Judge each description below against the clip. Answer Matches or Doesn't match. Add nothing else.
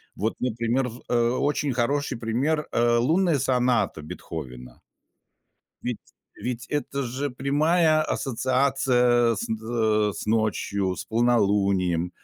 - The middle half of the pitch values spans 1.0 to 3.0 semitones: Doesn't match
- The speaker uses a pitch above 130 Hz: Doesn't match